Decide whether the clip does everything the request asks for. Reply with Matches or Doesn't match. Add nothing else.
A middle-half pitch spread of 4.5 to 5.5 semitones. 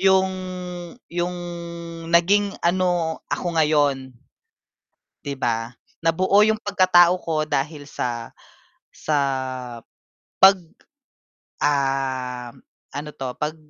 Matches